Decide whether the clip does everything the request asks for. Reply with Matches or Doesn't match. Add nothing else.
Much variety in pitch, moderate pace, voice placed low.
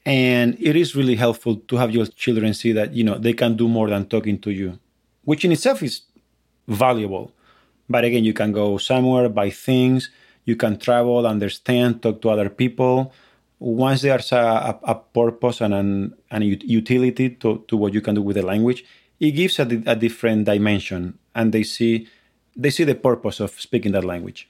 Doesn't match